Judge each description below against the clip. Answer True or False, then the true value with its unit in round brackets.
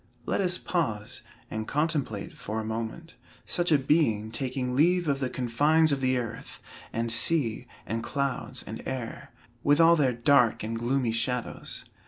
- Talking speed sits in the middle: True (160 wpm)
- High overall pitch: False (130 Hz)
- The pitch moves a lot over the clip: False (4.7 semitones)